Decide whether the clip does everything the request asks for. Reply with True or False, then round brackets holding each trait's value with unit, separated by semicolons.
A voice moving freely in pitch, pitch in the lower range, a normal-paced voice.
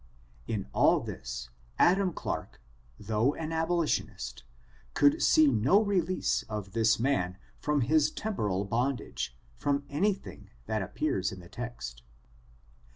False (8.1 semitones; 125 Hz; 120 wpm)